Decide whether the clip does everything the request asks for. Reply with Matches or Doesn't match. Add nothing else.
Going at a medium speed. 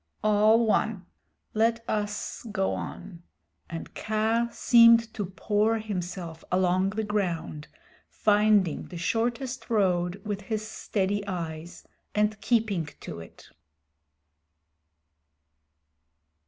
Doesn't match